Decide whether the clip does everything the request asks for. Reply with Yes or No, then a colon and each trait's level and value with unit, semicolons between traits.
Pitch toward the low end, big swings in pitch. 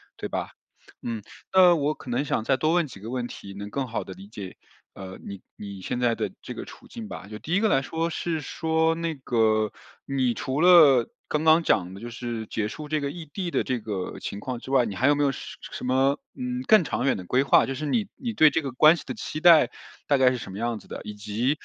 Yes: low, 130 Hz; wide, 6.2 semitones